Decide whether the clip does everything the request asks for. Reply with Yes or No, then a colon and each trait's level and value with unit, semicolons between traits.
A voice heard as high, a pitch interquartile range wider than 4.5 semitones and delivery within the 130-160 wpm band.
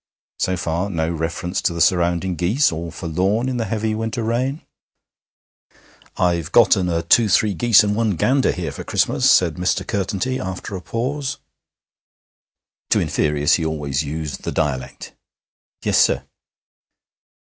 No: very low, 90 Hz; average, 5.3 semitones; average, 145 wpm